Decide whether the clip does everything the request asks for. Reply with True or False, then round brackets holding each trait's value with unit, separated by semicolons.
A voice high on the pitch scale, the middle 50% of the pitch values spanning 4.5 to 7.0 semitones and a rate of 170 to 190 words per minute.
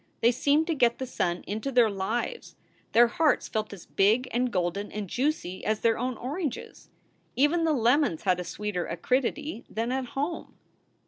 True (240 Hz; 5.0 semitones; 175 wpm)